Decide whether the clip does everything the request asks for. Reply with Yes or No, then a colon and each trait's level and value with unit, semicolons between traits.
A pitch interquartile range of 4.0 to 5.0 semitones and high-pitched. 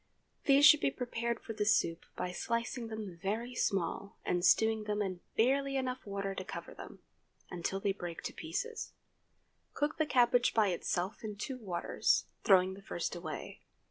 Yes: average, 4.6 semitones; high, 215 Hz